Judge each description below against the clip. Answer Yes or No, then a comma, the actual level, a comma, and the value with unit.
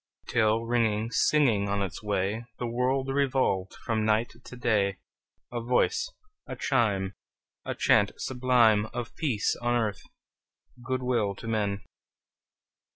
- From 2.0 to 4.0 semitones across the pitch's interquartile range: Yes, average, 3.3 semitones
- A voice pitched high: No, low, 115 Hz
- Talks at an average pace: No, slow, 130 wpm